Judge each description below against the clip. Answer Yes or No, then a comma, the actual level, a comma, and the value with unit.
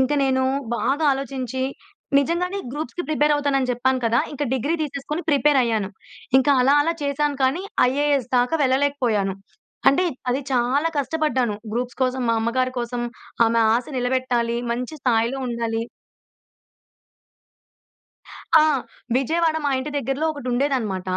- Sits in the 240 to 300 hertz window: Yes, very high, 260 Hz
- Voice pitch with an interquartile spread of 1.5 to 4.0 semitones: Yes, average, 3.0 semitones